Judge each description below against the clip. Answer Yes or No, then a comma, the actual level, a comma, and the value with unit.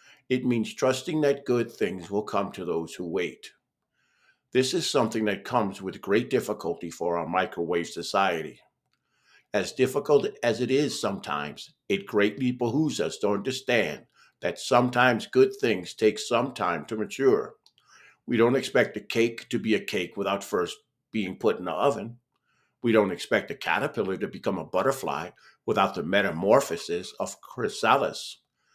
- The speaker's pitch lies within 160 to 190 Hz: No, low, 120 Hz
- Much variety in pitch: Yes, wide, 5.9 semitones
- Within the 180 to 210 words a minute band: No, average, 155 wpm